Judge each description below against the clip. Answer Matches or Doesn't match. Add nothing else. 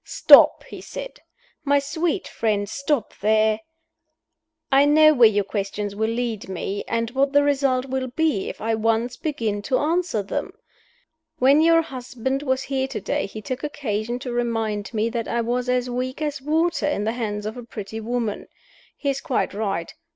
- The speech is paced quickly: Doesn't match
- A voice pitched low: Doesn't match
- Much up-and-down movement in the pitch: Doesn't match